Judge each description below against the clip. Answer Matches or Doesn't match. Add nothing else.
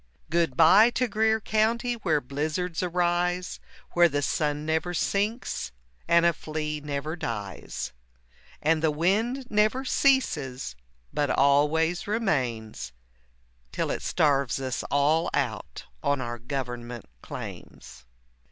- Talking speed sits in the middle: Doesn't match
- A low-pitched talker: Doesn't match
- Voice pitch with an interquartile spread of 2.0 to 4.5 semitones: Doesn't match